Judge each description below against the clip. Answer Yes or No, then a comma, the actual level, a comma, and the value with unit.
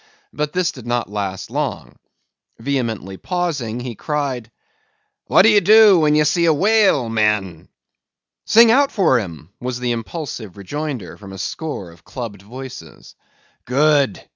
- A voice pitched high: No, low, 130 Hz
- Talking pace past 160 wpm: No, average, 145 wpm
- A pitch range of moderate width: No, wide, 6.8 semitones